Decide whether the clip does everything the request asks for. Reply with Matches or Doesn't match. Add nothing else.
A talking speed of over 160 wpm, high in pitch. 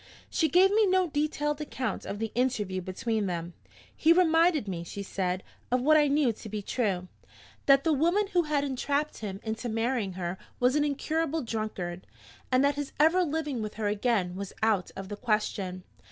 Matches